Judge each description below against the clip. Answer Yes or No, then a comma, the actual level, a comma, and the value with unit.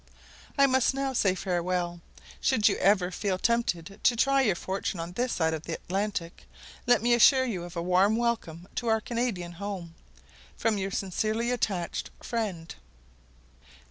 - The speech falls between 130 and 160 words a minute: Yes, average, 155 wpm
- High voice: Yes, high, 200 Hz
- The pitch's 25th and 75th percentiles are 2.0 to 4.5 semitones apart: No, average, 4.9 semitones